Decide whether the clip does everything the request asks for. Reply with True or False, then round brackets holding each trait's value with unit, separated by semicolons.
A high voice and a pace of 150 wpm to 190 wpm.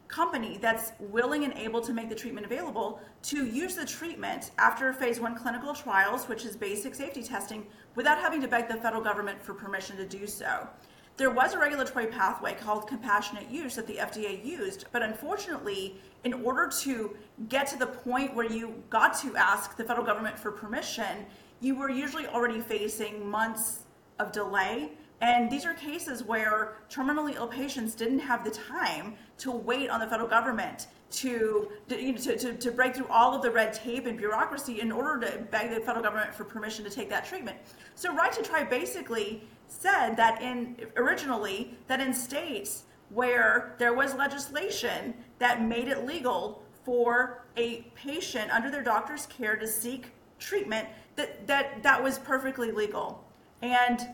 True (240 Hz; 175 wpm)